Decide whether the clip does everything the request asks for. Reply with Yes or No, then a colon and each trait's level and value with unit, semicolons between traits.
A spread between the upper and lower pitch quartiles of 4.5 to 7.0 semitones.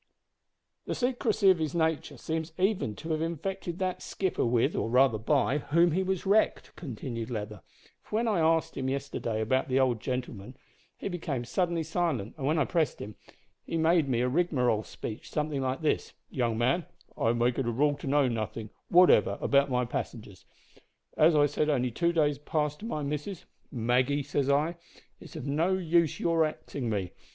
Yes: average, 5.1 semitones